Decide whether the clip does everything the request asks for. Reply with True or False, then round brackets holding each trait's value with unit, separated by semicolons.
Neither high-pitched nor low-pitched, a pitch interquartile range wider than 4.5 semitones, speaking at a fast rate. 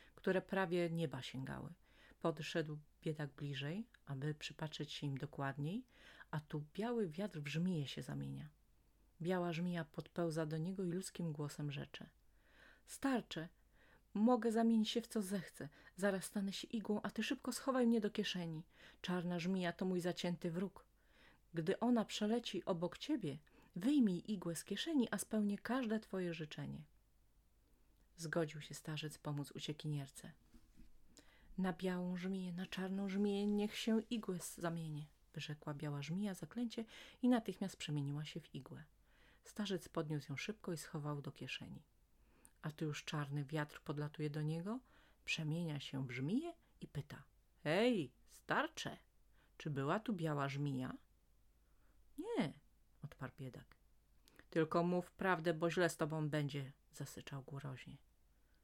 False (170 Hz; 5.3 semitones; 135 wpm)